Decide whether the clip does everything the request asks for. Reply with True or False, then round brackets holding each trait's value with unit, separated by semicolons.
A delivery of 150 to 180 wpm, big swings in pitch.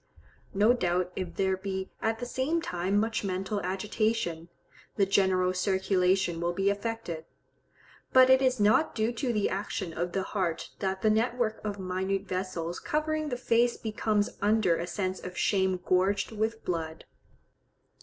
False (155 wpm; 3.4 semitones)